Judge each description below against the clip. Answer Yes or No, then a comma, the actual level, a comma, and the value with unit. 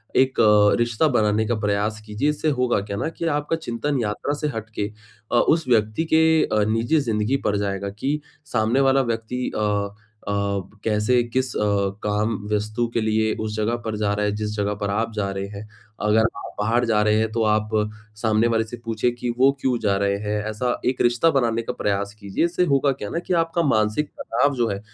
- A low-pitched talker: Yes, low, 110 Hz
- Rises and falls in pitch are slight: No, average, 3.1 semitones